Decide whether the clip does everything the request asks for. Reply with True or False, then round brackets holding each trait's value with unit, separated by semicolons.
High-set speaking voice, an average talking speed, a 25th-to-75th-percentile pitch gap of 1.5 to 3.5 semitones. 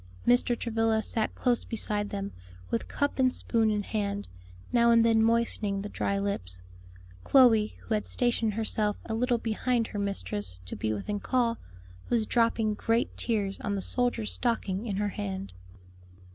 True (220 Hz; 160 wpm; 2.6 semitones)